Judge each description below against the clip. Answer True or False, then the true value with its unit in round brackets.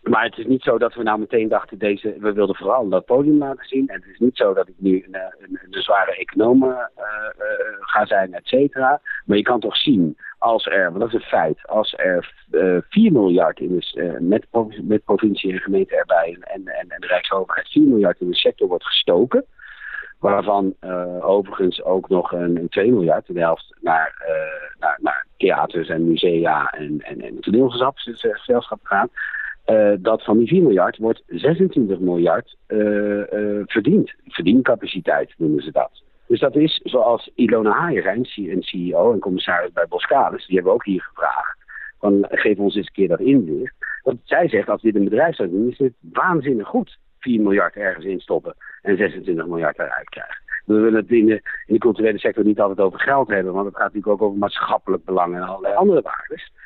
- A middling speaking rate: False (205 wpm)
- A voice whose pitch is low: True (110 Hz)